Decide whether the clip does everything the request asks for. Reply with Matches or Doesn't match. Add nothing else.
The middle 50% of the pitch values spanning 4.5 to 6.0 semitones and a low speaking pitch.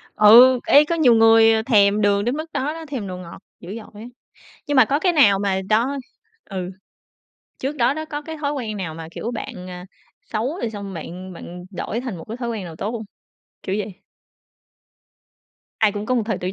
Doesn't match